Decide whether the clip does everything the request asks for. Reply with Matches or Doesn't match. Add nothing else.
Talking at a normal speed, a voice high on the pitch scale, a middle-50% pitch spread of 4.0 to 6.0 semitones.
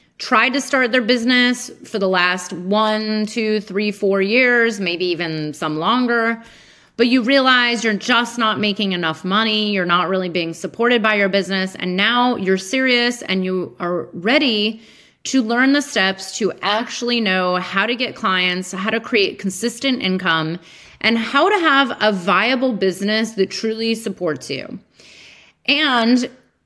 Matches